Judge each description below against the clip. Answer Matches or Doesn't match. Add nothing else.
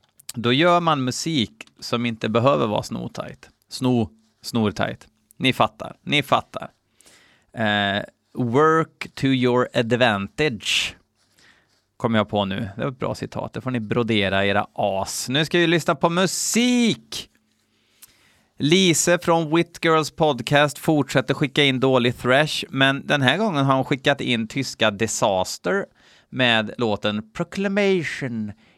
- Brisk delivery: Doesn't match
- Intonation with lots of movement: Matches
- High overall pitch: Doesn't match